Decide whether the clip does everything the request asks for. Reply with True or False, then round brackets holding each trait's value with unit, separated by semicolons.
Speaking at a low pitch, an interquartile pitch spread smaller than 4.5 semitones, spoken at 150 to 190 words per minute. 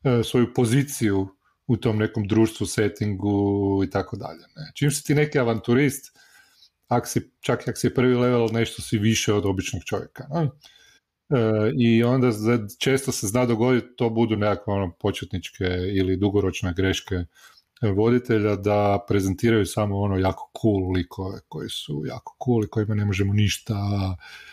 True (110 Hz; 3.5 semitones; 155 wpm)